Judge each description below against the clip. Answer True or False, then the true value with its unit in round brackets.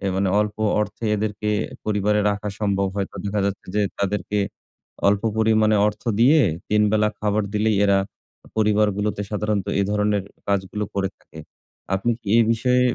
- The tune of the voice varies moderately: False (1.1 semitones)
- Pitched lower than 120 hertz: True (105 Hz)